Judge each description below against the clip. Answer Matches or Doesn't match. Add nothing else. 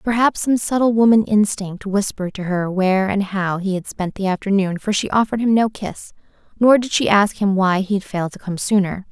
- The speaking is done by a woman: Matches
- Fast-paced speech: Matches